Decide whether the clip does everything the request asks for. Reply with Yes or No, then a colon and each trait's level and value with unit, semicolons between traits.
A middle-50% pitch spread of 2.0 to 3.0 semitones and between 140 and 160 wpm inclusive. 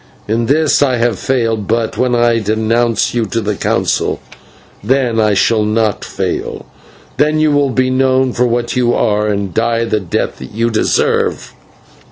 No: average, 2.7 semitones; average, 170 wpm